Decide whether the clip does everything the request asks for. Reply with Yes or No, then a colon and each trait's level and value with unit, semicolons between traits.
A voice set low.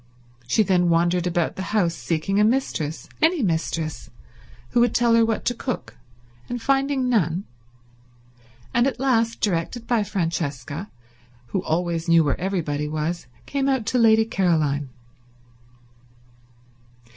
No: high, 190 Hz